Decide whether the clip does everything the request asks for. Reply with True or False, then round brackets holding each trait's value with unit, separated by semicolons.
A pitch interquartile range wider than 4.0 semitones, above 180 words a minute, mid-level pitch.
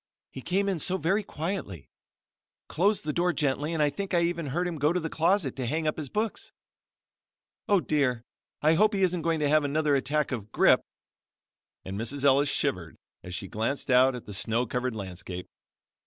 True (5.4 semitones; 195 wpm; 150 Hz)